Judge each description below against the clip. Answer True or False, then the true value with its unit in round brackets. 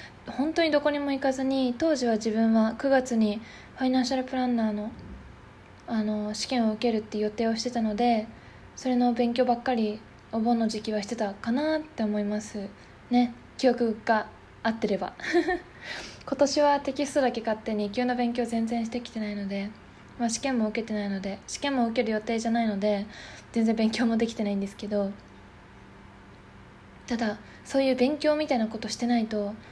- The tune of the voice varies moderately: True (3.0 semitones)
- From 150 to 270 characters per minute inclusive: False (350 characters per minute)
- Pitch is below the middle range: False (230 Hz)